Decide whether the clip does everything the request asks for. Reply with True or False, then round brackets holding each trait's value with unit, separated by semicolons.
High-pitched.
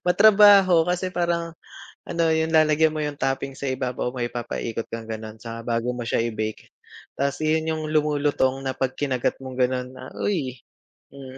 False (135 Hz)